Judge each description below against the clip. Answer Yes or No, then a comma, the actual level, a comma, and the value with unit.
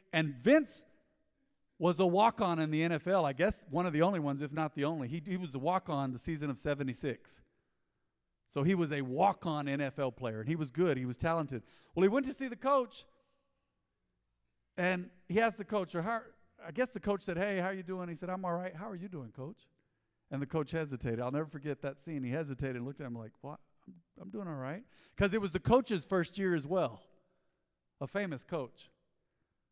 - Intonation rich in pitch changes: Yes, wide, 5.9 semitones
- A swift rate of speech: Yes, fast, 230 wpm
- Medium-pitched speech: Yes, medium, 165 Hz